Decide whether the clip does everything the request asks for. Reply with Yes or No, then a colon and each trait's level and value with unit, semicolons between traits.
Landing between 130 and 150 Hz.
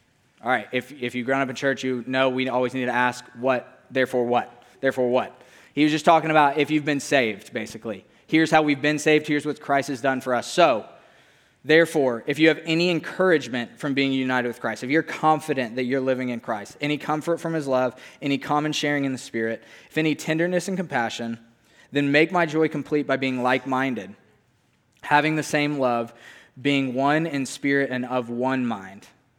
Yes: low, 135 Hz